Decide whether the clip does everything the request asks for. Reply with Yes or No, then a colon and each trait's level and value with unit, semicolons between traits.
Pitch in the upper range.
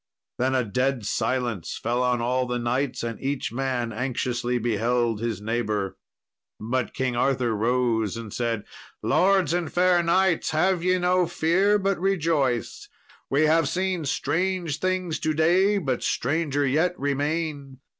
No: low, 135 Hz